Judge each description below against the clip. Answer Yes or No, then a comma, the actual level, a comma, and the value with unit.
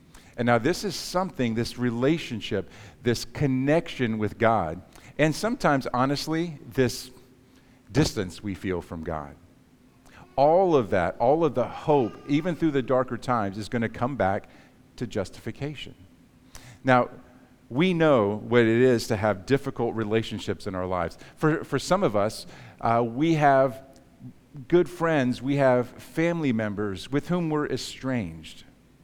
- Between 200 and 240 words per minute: No, average, 145 wpm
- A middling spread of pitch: Yes, average, 4.5 semitones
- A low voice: Yes, low, 125 Hz